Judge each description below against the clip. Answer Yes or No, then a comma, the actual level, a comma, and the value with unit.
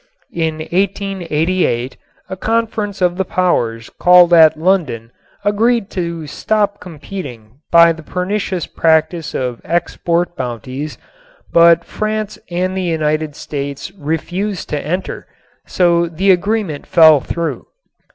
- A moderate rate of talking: No, slow, 115 wpm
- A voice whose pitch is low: No, medium, 170 Hz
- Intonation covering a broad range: No, average, 3.7 semitones